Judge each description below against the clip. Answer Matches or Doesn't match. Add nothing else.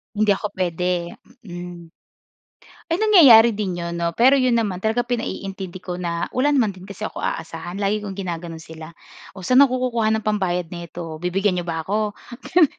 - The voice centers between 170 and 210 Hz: Matches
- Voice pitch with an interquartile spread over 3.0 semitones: Matches